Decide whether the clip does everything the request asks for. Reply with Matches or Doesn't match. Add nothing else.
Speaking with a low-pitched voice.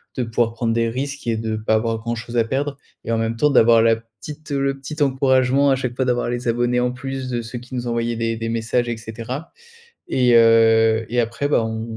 Matches